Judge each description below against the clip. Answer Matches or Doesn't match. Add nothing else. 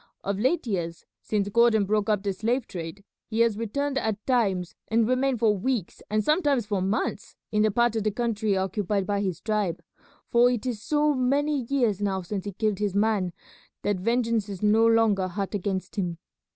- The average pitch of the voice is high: Matches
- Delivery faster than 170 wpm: Matches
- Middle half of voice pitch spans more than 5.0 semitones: Doesn't match